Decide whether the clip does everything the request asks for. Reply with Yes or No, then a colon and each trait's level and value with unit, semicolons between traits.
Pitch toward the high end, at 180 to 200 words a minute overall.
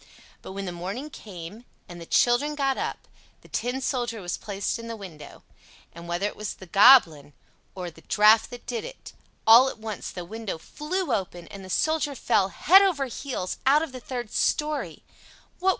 Yes: high, 225 Hz; average, 185 wpm